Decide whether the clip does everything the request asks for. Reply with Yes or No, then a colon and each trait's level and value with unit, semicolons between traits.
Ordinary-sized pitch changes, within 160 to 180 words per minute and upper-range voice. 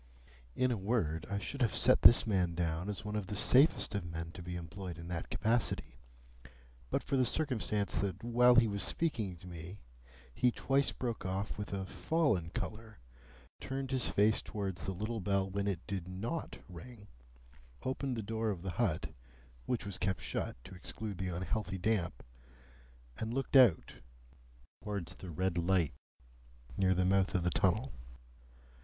No: average, 4.1 semitones; average, 170 wpm; low, 100 Hz